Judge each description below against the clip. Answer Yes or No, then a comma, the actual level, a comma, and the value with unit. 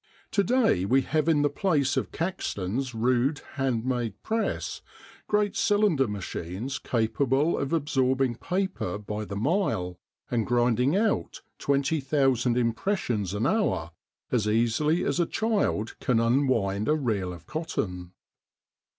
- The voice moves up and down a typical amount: No, wide, 6.0 semitones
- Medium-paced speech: No, slow, 130 wpm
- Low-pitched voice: Yes, low, 130 Hz